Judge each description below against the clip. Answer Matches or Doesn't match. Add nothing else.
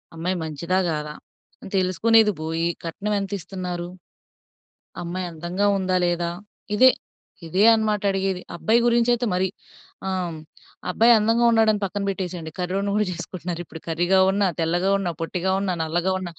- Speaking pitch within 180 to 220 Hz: Matches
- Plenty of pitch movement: Doesn't match